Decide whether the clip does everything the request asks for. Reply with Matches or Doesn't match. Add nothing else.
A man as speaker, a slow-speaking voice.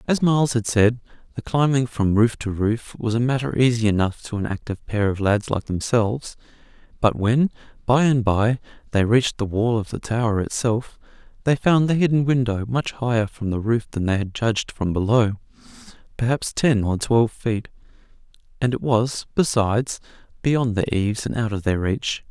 Doesn't match